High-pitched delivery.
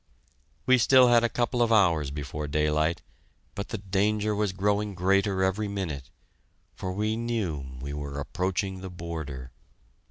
No: very low, 95 Hz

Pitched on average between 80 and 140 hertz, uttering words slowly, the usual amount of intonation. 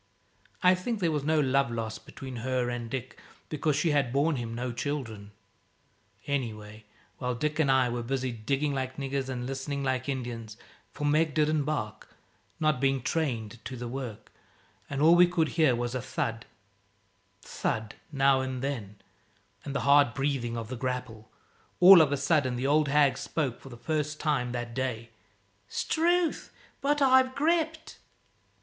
No: low, 135 Hz; average, 165 wpm; average, 3.9 semitones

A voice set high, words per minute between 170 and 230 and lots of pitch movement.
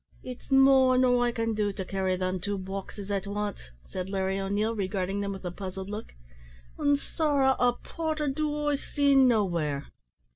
Yes: high, 210 Hz; average, 175 wpm; wide, 5.7 semitones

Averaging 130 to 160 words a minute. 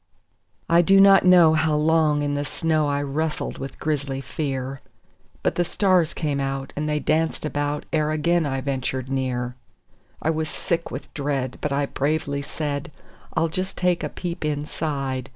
No: average, 170 wpm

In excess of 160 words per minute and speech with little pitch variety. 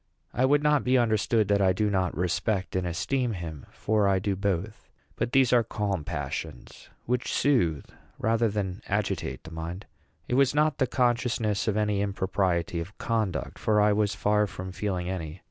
No: average, 180 wpm; average, 3.9 semitones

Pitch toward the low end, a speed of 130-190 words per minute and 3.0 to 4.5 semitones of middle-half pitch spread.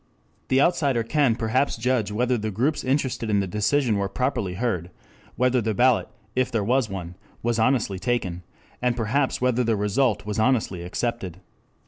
Yes: low, 115 Hz; average, 165 wpm; average, 3.7 semitones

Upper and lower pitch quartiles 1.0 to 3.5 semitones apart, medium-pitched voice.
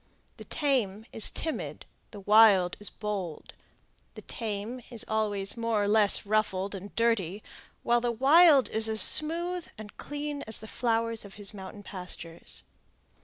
No: average, 2.9 semitones; high, 220 Hz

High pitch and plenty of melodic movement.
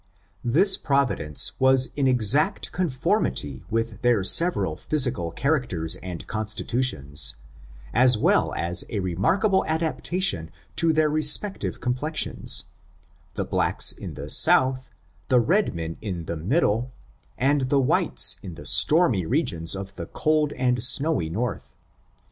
No: low, 125 Hz; wide, 9.0 semitones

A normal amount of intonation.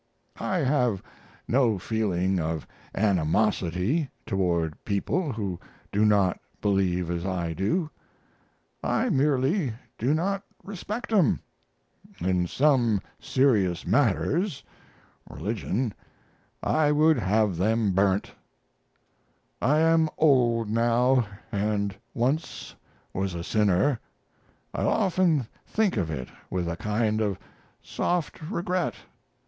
No: wide, 7.7 semitones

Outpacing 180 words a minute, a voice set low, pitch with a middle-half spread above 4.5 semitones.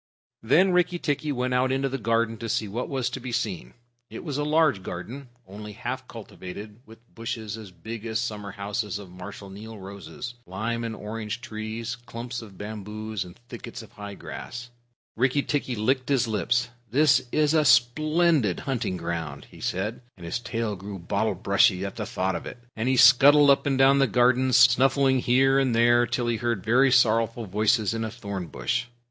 No: average, 190 wpm; low, 115 Hz; average, 3.7 semitones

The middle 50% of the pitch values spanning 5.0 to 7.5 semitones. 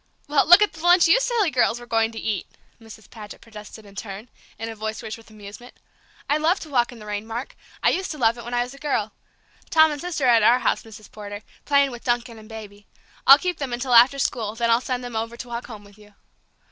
No: average, 4.1 semitones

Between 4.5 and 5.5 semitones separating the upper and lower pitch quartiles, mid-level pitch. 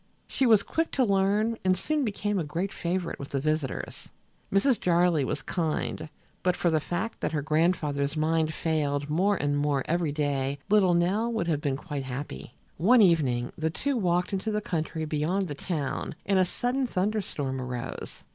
Yes: average, 5.1 semitones; medium, 170 Hz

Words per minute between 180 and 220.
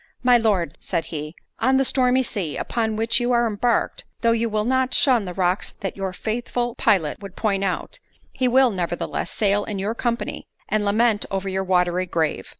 Yes: average, 190 wpm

